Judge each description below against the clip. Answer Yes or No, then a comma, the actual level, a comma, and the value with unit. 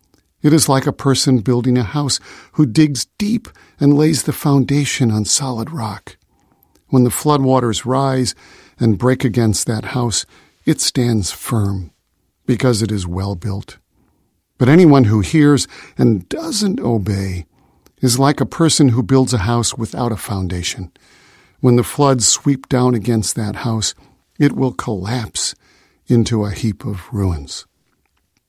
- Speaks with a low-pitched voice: Yes, low, 120 Hz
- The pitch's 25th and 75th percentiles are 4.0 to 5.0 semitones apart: Yes, average, 4.7 semitones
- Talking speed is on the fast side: No, average, 145 wpm